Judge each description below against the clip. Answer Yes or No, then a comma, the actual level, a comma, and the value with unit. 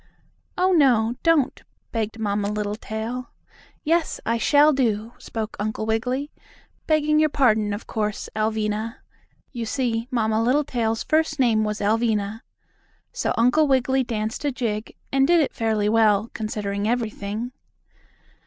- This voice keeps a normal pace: No, slow, 130 wpm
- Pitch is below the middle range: No, high, 225 Hz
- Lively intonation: No, average, 3.5 semitones